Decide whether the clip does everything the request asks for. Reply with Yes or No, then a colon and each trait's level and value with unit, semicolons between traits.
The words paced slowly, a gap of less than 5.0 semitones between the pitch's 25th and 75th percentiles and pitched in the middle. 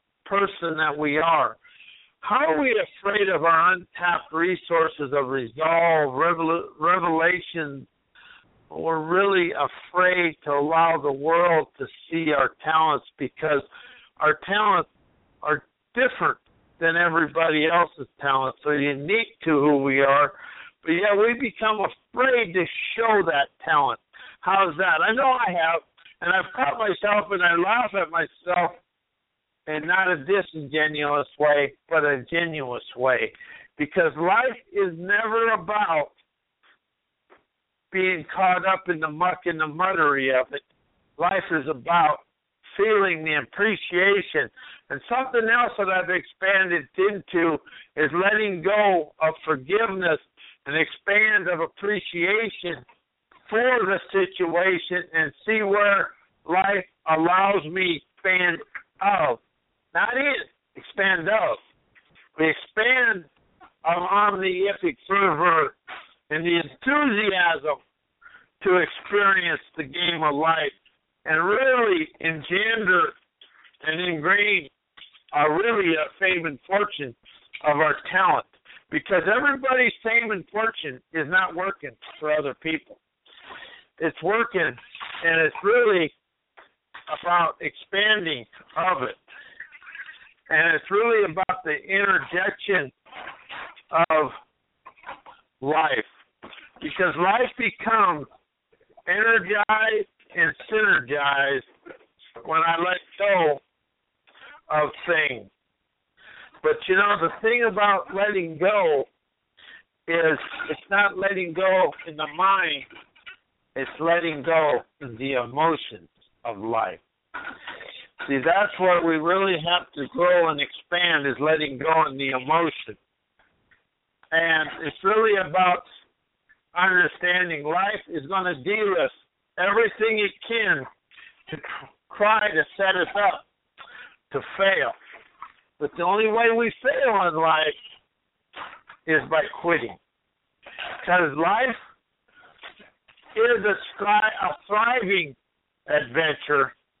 Yes: slow, 115 wpm; average, 4.5 semitones; medium, 180 Hz